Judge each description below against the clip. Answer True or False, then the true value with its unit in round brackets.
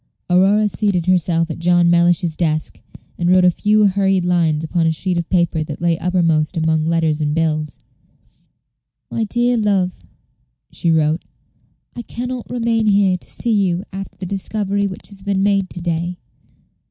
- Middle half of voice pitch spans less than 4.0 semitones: True (3.3 semitones)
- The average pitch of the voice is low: False (180 Hz)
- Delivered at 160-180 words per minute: True (165 wpm)